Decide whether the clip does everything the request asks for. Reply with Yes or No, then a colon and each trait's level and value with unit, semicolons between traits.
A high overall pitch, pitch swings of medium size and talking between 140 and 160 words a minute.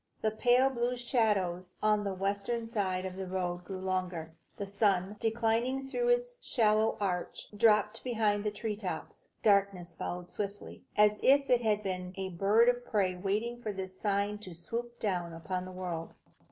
No: high, 205 Hz; average, 3.5 semitones; average, 170 wpm